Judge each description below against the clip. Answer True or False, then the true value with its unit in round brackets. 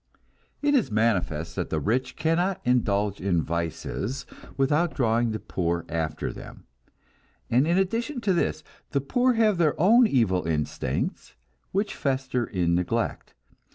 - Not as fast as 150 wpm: True (140 wpm)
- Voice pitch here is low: True (125 Hz)